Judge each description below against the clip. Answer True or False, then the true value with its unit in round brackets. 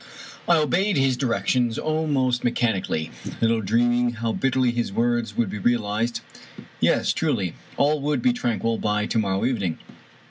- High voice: False (120 Hz)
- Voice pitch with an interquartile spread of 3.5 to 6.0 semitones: False (3.0 semitones)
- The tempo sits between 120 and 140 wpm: False (155 wpm)